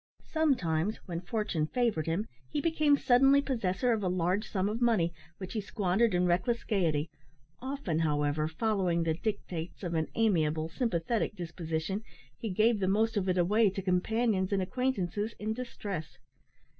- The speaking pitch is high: Yes, high, 195 Hz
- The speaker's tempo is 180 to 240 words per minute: No, average, 155 wpm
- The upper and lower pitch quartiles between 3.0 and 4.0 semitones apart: No, average, 5.0 semitones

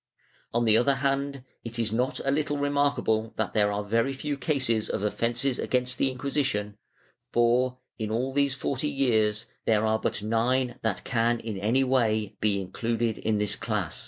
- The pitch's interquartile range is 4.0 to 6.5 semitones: No, average, 3.6 semitones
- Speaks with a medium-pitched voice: No, low, 120 Hz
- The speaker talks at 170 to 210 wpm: Yes, average, 175 wpm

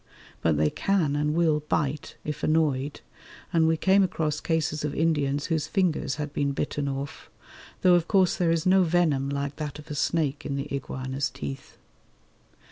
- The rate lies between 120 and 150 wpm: No, average, 175 wpm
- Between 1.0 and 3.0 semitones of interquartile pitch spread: Yes, narrow, 2.6 semitones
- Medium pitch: Yes, medium, 150 Hz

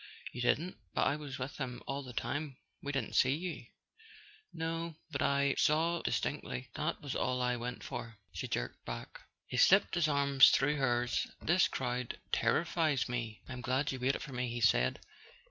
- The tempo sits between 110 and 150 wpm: No, average, 180 wpm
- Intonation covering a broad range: No, average, 3.5 semitones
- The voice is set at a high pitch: No, low, 135 Hz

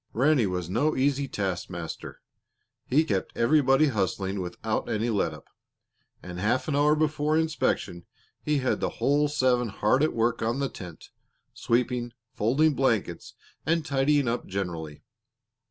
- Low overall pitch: Yes, low, 125 Hz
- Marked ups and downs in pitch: Yes, wide, 6.7 semitones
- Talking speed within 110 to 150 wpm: Yes, average, 140 wpm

